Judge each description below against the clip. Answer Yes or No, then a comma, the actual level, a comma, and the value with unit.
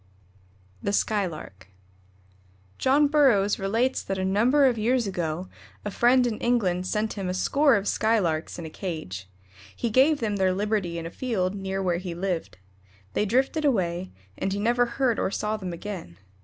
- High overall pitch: Yes, high, 200 Hz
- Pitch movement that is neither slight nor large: Yes, average, 4.7 semitones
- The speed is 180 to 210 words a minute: No, average, 170 wpm